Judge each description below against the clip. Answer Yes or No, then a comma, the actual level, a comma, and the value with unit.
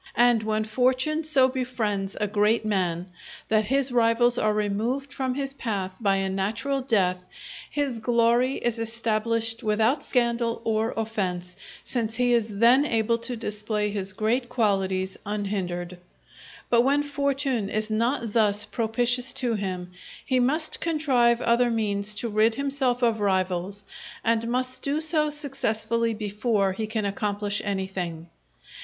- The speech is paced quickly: No, average, 140 wpm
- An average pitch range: Yes, average, 3.3 semitones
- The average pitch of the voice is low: No, high, 225 Hz